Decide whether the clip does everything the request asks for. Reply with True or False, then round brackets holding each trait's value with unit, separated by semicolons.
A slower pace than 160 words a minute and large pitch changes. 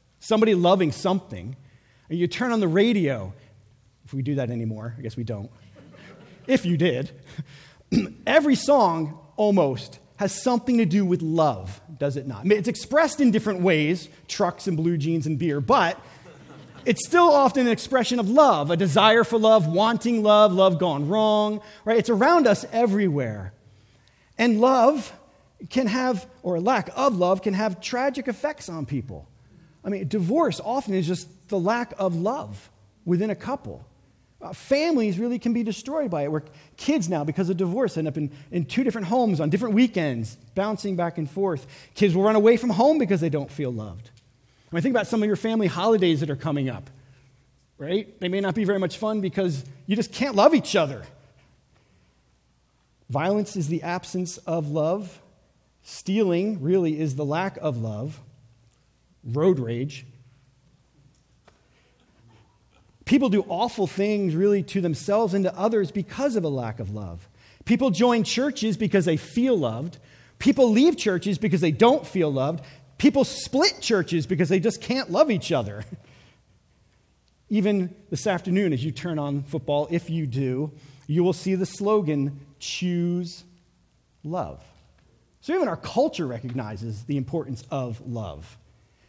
False (165 wpm; 7.4 semitones)